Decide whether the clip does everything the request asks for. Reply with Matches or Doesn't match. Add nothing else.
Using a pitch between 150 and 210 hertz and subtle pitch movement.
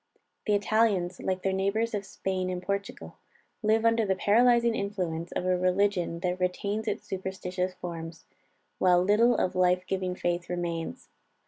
Matches